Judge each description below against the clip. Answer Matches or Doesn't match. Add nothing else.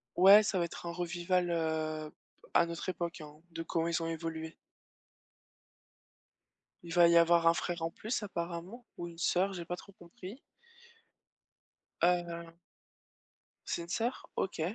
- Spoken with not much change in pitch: Matches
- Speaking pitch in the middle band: Matches